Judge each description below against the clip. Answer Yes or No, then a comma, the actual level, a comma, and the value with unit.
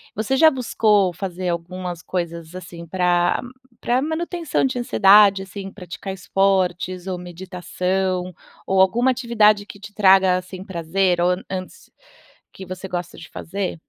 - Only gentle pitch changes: Yes, narrow, 2.2 semitones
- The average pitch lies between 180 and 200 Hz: Yes, high, 190 Hz